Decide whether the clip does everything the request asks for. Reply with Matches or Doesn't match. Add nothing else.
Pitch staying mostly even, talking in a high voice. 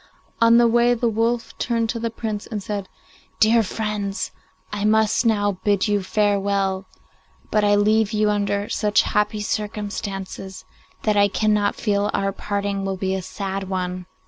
Matches